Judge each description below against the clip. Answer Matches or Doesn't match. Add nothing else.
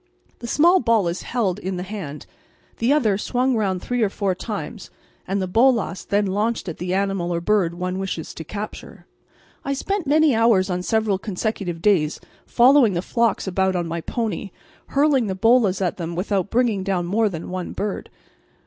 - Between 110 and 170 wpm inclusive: Doesn't match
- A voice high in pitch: Matches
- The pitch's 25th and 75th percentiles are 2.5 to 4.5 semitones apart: Matches